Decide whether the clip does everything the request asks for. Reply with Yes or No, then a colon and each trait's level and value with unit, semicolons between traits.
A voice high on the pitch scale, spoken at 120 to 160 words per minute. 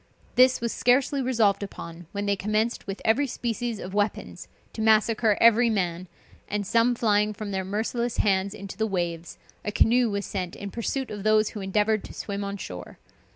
No: high, 210 Hz; average, 185 wpm